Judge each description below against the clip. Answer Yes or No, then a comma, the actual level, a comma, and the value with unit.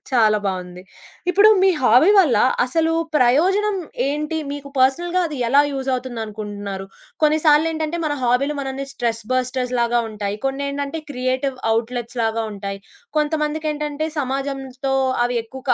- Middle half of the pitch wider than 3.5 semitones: Yes, average, 4.1 semitones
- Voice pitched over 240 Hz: Yes, very high, 270 Hz